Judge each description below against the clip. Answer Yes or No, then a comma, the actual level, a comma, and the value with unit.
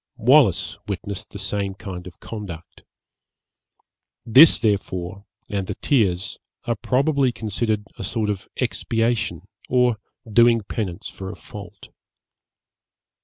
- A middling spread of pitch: Yes, average, 3.4 semitones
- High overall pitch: No, low, 105 Hz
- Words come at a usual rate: No, slow, 115 wpm